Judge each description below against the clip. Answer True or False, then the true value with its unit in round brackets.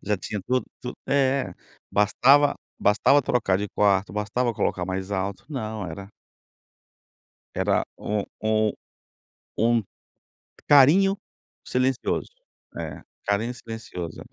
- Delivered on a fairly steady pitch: False (4.3 semitones)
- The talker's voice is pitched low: True (110 Hz)